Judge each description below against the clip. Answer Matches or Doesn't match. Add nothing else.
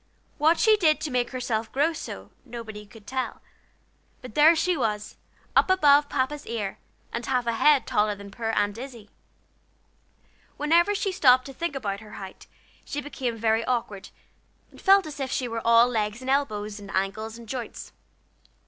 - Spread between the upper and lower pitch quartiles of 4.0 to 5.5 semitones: Matches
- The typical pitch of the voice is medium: Doesn't match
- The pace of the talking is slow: Doesn't match